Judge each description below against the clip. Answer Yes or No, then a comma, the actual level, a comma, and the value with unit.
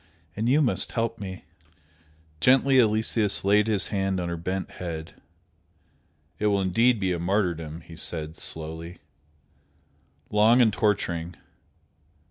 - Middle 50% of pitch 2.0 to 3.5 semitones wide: No, average, 4.2 semitones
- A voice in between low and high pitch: No, very low, 95 Hz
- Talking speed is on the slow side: Yes, slow, 125 wpm